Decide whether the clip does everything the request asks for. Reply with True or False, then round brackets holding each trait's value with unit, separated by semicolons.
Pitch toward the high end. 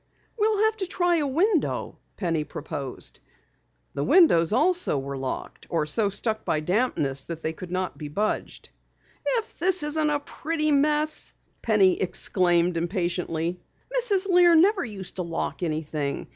True (205 Hz)